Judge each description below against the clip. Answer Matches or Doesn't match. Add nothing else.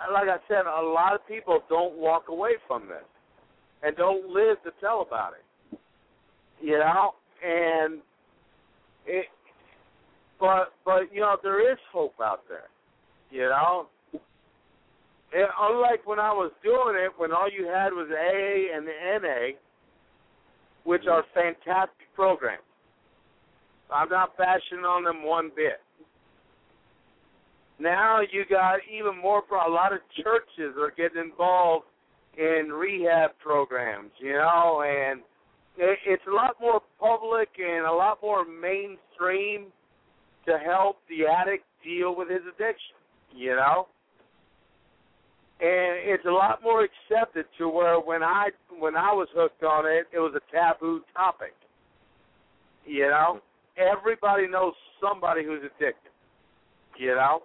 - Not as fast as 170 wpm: Matches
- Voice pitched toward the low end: Doesn't match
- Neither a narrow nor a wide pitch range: Matches